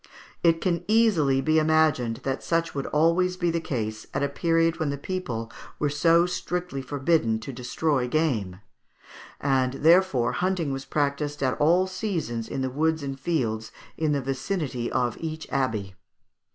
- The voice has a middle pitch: Yes, medium, 145 Hz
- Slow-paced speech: No, average, 160 wpm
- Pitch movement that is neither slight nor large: Yes, average, 4.2 semitones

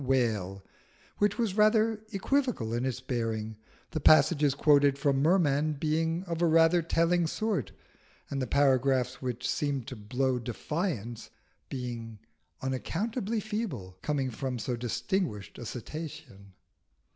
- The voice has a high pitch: No, medium, 140 Hz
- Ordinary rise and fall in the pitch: No, wide, 5.7 semitones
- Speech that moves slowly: Yes, slow, 125 wpm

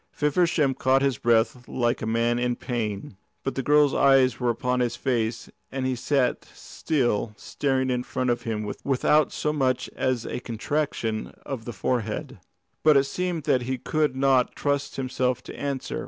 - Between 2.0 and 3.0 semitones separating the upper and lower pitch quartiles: Yes, narrow, 2.6 semitones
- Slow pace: No, average, 170 wpm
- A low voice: Yes, low, 130 Hz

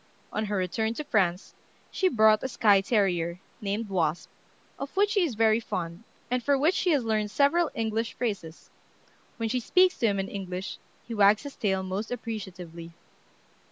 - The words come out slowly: No, average, 175 wpm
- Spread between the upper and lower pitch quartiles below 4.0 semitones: No, average, 4.4 semitones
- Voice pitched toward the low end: No, high, 215 Hz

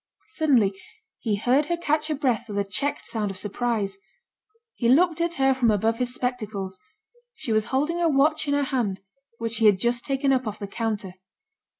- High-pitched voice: Yes, high, 245 Hz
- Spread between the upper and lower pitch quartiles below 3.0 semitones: No, average, 5.2 semitones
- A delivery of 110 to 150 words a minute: No, average, 195 wpm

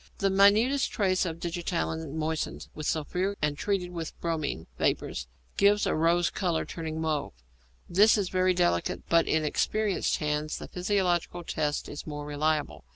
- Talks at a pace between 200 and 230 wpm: No, average, 155 wpm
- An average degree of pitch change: Yes, average, 3.4 semitones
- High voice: No, medium, 170 Hz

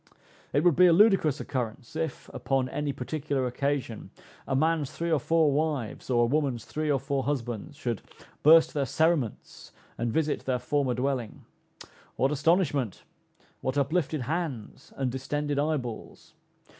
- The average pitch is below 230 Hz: Yes, medium, 140 Hz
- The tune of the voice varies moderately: Yes, average, 3.4 semitones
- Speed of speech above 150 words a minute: No, average, 145 wpm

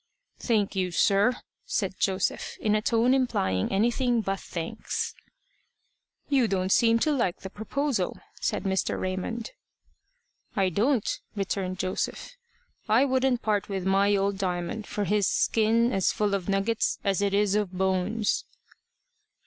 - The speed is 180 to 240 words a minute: No, average, 140 wpm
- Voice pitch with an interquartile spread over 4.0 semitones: No, average, 3.2 semitones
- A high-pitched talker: Yes, high, 205 Hz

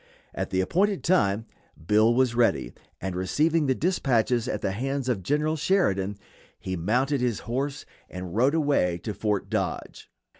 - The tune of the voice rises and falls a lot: Yes, wide, 6.6 semitones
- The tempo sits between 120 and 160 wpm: Yes, average, 155 wpm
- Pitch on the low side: Yes, low, 120 Hz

